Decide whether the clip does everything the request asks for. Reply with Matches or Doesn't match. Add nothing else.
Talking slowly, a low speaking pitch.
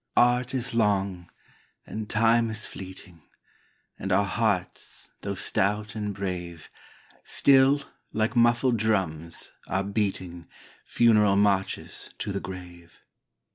Matches